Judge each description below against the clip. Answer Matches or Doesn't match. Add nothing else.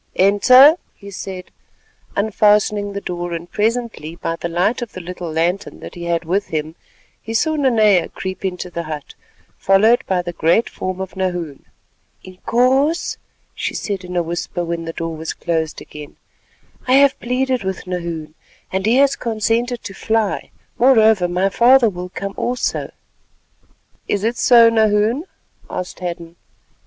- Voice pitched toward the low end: Doesn't match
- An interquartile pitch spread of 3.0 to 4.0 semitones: Doesn't match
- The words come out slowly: Doesn't match